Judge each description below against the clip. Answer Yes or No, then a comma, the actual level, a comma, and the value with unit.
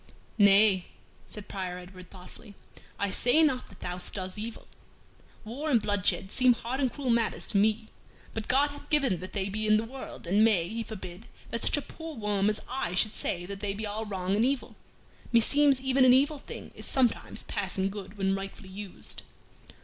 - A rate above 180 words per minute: Yes, average, 195 wpm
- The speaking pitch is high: Yes, high, 215 Hz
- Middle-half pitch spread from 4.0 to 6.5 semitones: Yes, average, 4.4 semitones